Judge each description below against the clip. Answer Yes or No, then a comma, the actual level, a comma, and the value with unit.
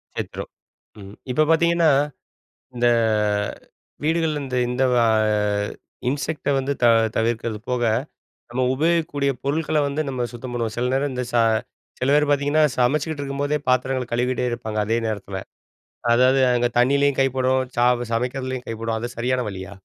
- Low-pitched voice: Yes, low, 130 Hz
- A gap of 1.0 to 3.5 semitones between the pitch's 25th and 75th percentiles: Yes, average, 2.9 semitones